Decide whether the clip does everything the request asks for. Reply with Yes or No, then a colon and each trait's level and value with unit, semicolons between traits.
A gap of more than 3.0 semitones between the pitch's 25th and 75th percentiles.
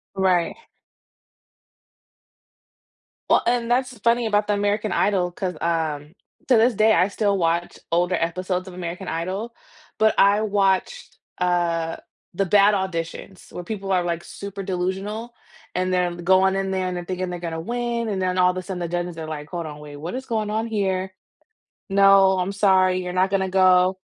No: narrow, 2.5 semitones